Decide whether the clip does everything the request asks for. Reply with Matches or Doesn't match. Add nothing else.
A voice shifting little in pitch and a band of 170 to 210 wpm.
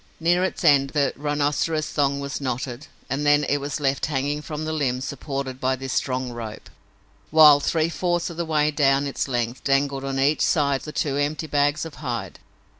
Matches